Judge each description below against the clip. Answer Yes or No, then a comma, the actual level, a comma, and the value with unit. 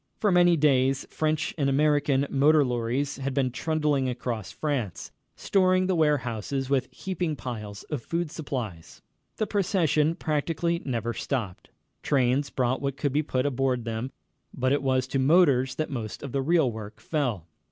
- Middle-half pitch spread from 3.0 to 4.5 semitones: Yes, average, 3.6 semitones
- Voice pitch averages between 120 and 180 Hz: Yes, medium, 140 Hz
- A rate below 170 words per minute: Yes, average, 160 wpm